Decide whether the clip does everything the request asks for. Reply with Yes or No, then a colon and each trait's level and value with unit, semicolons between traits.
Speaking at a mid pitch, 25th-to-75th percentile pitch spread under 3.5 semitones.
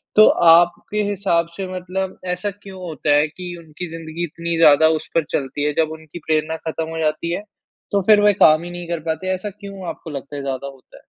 Yes: medium, 170 Hz; average, 3.1 semitones